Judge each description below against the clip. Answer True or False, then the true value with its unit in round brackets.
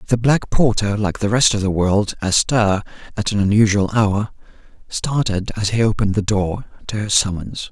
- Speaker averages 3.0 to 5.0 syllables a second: True (4.9 syllables/s)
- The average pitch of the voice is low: True (105 Hz)